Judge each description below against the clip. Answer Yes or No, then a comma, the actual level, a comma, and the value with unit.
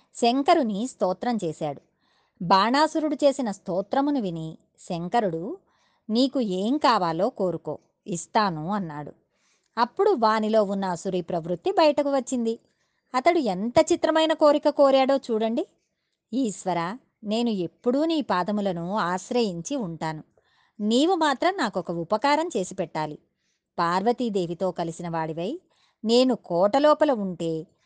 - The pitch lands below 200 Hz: No, high, 220 Hz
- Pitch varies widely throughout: Yes, wide, 7.4 semitones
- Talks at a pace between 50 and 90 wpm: No, average, 100 wpm